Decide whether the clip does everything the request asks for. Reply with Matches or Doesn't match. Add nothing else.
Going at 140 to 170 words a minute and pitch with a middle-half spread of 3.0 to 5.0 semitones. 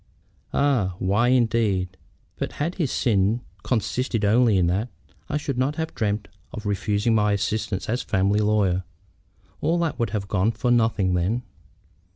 Matches